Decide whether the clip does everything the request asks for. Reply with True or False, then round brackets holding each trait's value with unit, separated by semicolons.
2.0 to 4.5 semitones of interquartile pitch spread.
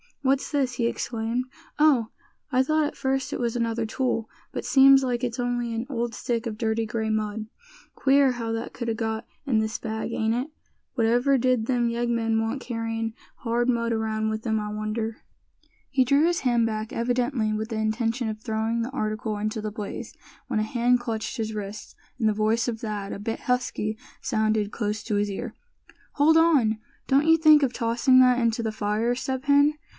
True (2.4 semitones)